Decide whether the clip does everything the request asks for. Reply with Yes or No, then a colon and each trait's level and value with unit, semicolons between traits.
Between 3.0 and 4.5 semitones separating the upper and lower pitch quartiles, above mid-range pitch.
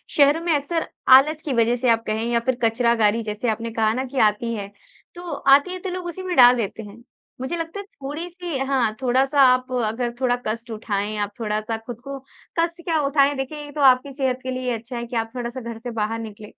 Yes: average, 3.9 semitones; very high, 250 Hz